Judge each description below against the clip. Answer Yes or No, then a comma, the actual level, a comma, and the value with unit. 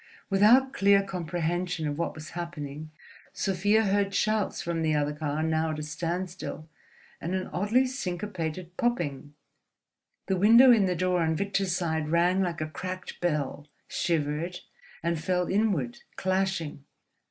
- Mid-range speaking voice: Yes, medium, 175 Hz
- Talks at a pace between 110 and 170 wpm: Yes, average, 140 wpm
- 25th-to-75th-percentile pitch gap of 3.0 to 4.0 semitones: Yes, average, 3.5 semitones